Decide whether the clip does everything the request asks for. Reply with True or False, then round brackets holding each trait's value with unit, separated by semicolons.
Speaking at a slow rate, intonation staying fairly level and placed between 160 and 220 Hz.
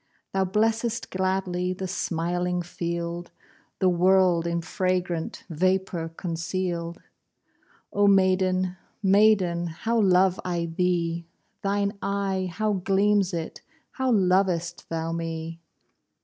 True (105 wpm; 2.1 semitones; 185 Hz)